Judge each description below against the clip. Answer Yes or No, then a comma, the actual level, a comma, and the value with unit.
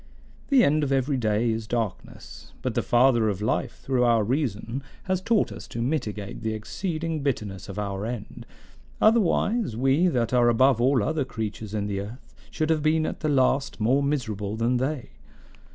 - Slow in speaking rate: No, average, 180 wpm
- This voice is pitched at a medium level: No, low, 125 Hz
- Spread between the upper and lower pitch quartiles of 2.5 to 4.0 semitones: No, average, 5.3 semitones